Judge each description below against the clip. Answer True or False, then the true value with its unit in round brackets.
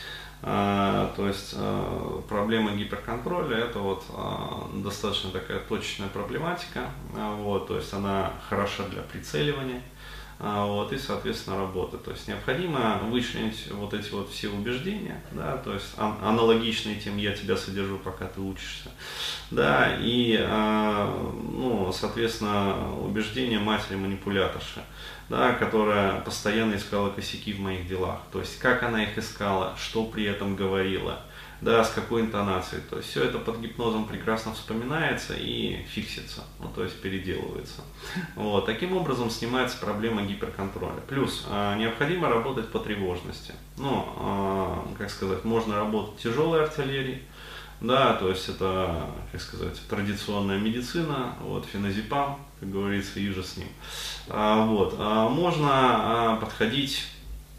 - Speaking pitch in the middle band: False (105 Hz)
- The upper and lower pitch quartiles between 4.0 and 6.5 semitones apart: False (2.7 semitones)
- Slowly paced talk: False (130 wpm)